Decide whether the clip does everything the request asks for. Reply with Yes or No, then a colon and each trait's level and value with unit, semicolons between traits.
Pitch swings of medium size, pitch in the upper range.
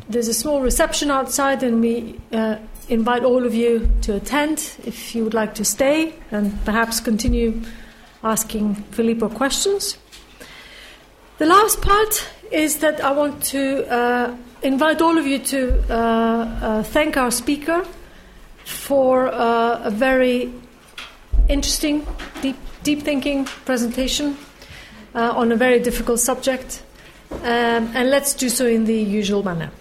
Yes: average, 3.6 semitones; high, 245 Hz